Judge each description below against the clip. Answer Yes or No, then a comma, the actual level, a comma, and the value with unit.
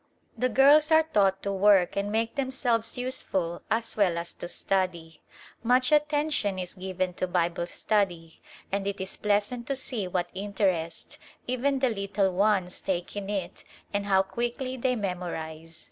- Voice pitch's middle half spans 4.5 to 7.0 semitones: Yes, average, 5.0 semitones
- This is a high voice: Yes, high, 200 Hz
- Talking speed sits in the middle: Yes, average, 160 wpm